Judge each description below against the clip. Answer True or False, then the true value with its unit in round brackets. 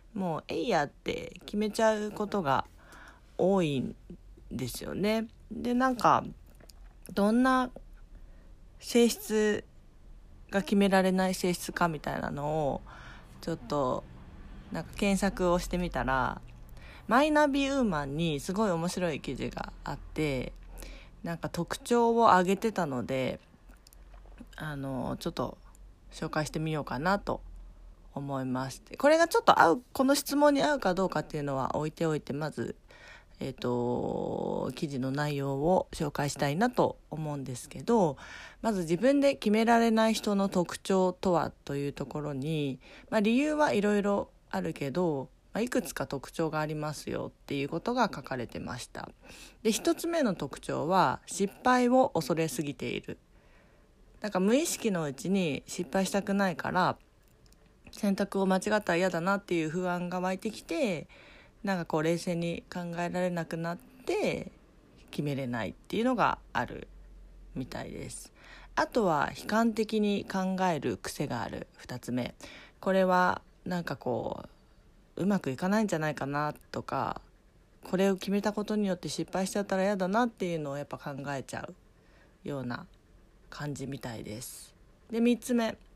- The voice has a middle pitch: True (180 Hz)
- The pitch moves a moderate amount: False (6.5 semitones)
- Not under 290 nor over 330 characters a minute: True (300 characters per minute)